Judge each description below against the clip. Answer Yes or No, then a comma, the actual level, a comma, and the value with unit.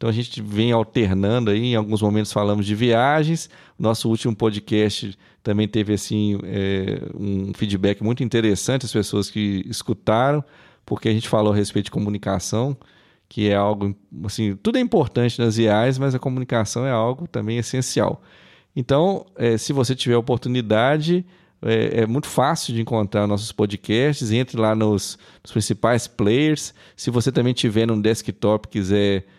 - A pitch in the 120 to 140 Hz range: No, low, 110 Hz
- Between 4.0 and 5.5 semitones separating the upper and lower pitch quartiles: No, average, 3.2 semitones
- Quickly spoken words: No, average, 165 wpm